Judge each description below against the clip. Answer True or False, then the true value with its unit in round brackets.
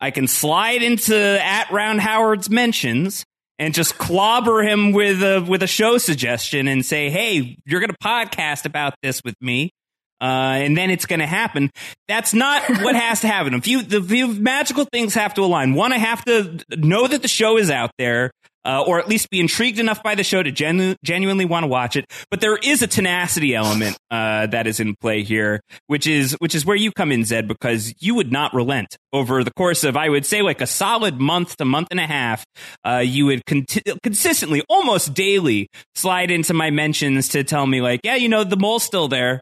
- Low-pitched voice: False (170 Hz)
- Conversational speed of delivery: False (215 wpm)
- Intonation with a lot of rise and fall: True (8.1 semitones)